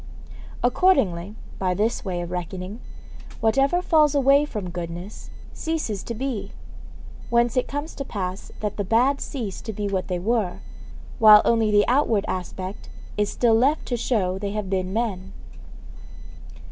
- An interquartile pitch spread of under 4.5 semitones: No, average, 4.8 semitones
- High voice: Yes, high, 215 Hz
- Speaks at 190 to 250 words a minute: No, average, 150 wpm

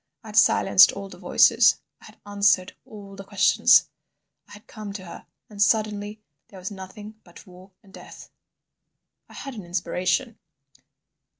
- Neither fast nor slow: Yes, average, 155 wpm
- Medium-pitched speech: No, high, 200 Hz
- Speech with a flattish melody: Yes, narrow, 1.9 semitones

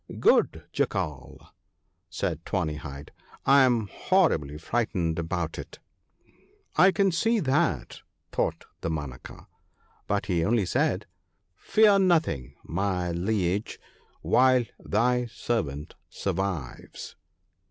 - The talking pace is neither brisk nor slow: No, slow, 105 wpm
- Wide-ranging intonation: Yes, wide, 8.0 semitones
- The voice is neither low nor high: No, low, 100 Hz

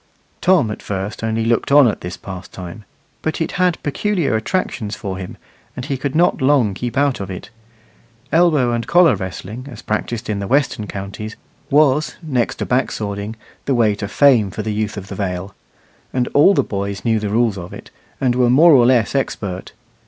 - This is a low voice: Yes, low, 115 Hz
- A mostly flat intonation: No, wide, 5.4 semitones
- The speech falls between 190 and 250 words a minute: Yes, average, 195 wpm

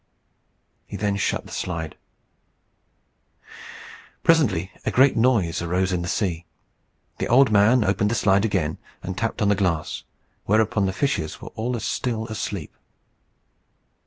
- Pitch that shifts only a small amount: No, average, 3.9 semitones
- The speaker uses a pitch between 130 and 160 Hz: No, low, 100 Hz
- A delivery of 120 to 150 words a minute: Yes, average, 145 wpm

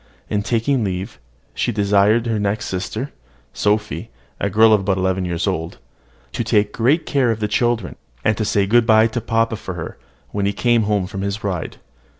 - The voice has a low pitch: Yes, low, 105 Hz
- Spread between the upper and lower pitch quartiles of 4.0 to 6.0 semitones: No, narrow, 2.5 semitones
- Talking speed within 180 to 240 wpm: Yes, average, 185 wpm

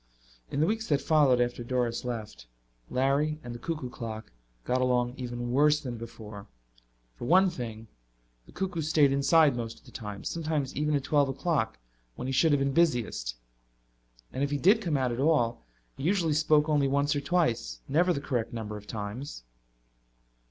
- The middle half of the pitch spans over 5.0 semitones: No, average, 4.4 semitones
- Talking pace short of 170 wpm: No, average, 180 wpm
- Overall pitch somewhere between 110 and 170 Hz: Yes, low, 135 Hz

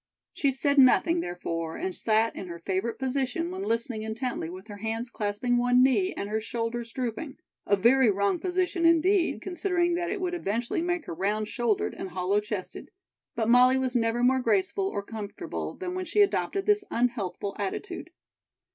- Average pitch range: No, wide, 8.1 semitones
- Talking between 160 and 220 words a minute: Yes, average, 175 wpm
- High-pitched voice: Yes, high, 240 Hz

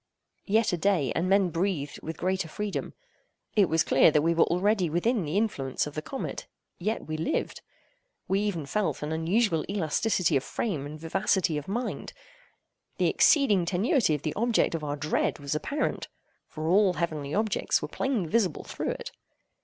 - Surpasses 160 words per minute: Yes, average, 175 wpm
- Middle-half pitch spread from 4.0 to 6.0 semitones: Yes, average, 5.1 semitones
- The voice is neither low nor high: Yes, medium, 180 Hz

